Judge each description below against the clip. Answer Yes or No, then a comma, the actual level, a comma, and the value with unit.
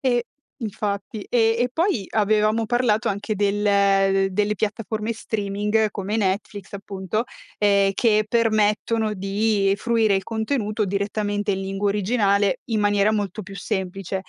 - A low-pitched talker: No, high, 210 Hz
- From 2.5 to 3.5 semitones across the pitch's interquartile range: No, narrow, 1.8 semitones